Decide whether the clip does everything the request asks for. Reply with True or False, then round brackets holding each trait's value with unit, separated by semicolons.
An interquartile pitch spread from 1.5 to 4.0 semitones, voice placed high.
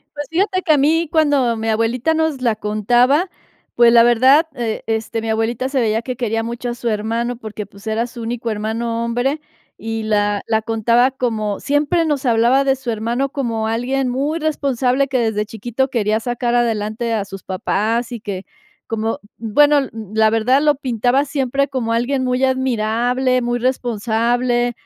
True (3.0 semitones; 240 Hz)